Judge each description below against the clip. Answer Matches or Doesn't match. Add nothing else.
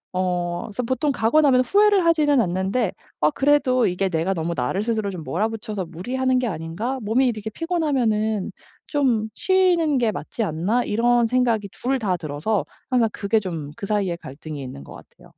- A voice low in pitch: Doesn't match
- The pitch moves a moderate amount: Doesn't match